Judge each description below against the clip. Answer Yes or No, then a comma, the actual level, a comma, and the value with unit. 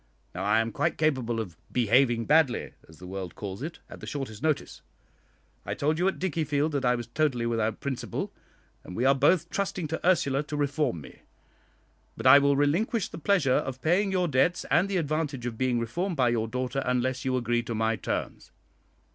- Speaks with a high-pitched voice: No, low, 135 Hz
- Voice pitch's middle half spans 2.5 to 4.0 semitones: No, average, 4.8 semitones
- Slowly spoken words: No, average, 195 wpm